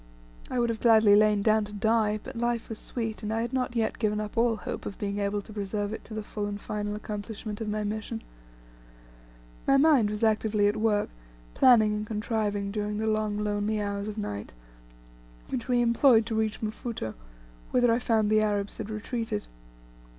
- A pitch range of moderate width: No, narrow, 1.6 semitones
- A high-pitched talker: Yes, high, 215 Hz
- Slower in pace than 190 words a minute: No, average, 195 wpm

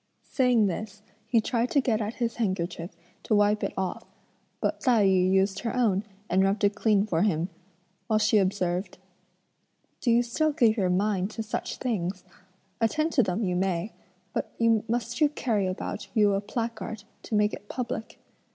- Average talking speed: Yes, average, 175 wpm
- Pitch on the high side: Yes, high, 210 Hz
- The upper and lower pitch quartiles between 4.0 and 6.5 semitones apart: No, average, 3.4 semitones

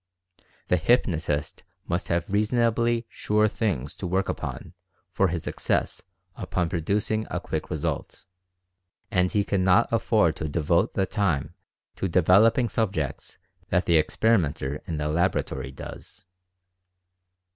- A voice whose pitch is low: Yes, very low, 90 Hz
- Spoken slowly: Yes, slow, 130 wpm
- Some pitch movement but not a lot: Yes, average, 4.7 semitones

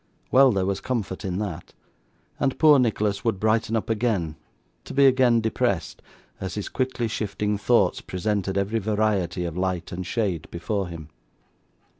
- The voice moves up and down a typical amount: Yes, average, 3.6 semitones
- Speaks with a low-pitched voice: Yes, low, 105 Hz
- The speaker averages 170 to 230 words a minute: No, average, 155 wpm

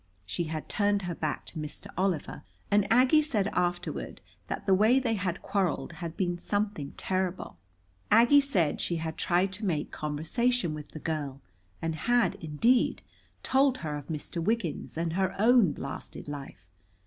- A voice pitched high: No, medium, 180 Hz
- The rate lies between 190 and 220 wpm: No, average, 160 wpm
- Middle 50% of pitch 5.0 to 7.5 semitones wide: Yes, wide, 5.4 semitones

